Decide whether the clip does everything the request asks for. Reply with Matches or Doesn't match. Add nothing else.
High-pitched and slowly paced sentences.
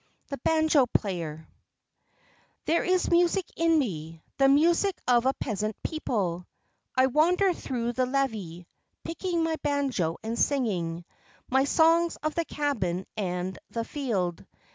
Matches